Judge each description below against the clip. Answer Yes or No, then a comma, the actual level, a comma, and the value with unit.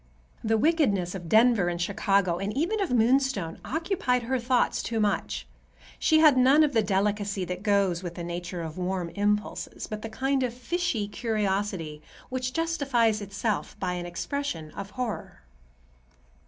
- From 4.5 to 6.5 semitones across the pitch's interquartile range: Yes, wide, 5.4 semitones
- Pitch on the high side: Yes, high, 210 Hz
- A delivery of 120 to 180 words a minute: Yes, average, 160 wpm